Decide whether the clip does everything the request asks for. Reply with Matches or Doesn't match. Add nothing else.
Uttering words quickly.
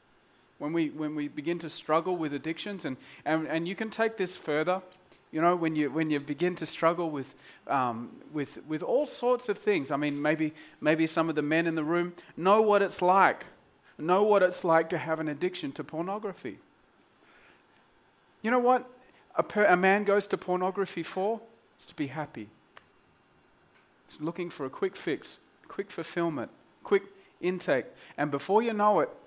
Doesn't match